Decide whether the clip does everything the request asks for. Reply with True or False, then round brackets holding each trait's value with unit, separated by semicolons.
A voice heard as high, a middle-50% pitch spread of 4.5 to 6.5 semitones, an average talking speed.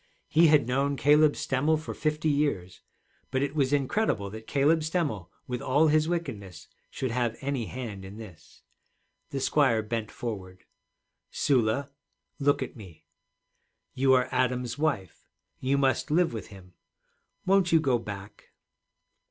False (130 Hz; 5.2 semitones; 145 wpm)